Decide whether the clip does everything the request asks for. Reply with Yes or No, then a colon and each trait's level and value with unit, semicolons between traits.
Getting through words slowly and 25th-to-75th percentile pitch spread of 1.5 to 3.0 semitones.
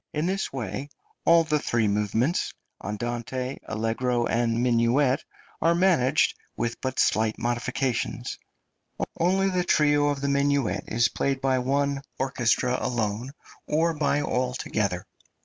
No: slow, 130 wpm; average, 3.6 semitones